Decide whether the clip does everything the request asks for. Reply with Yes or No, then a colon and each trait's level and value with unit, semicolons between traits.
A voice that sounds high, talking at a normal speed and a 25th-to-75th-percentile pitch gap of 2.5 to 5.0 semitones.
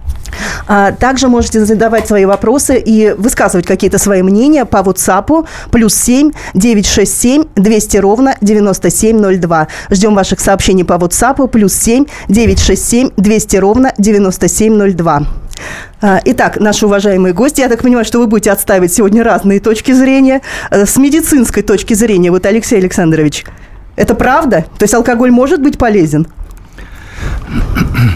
Yes: high, 210 Hz; average, 125 wpm; average, 3.7 semitones